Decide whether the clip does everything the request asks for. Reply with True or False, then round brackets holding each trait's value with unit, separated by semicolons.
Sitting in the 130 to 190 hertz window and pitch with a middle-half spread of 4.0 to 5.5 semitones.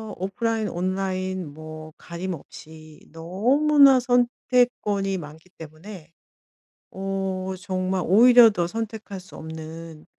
True (185 Hz; 5.1 semitones)